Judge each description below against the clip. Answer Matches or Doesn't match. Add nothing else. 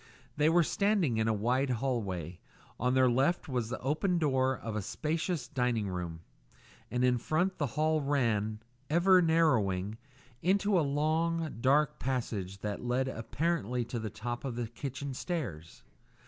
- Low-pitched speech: Matches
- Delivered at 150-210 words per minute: Matches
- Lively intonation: Matches